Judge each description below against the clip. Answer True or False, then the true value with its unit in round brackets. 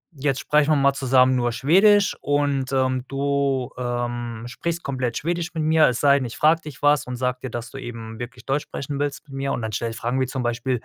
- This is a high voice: False (135 Hz)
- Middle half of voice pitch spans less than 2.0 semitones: False (2.9 semitones)